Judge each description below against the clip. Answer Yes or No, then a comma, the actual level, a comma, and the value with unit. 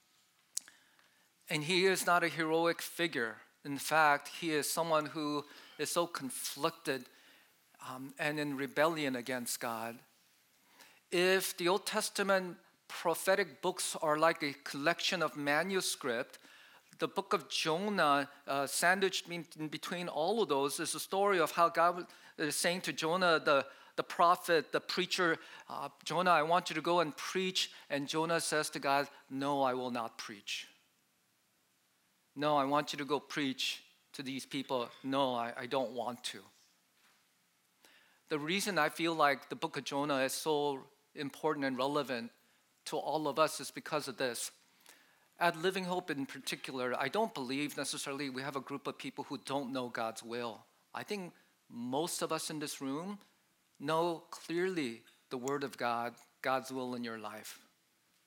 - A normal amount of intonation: Yes, average, 3.8 semitones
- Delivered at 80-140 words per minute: No, average, 160 wpm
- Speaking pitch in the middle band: Yes, medium, 150 Hz